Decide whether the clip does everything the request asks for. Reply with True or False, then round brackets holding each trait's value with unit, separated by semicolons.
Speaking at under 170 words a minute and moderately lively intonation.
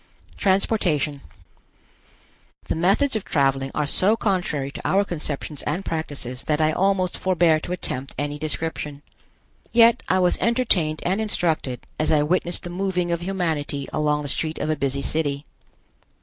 True (150 wpm; 4.2 semitones)